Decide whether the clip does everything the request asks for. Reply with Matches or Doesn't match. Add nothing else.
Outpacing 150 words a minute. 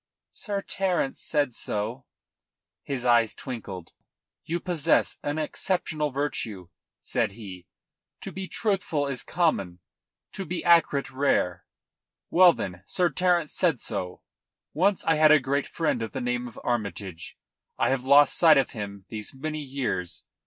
Doesn't match